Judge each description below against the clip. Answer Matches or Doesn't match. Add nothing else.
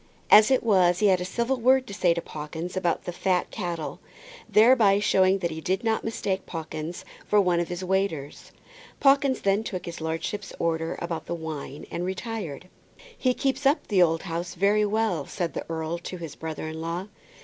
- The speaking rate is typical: Matches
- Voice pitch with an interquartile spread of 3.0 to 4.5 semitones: Matches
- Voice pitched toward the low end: Doesn't match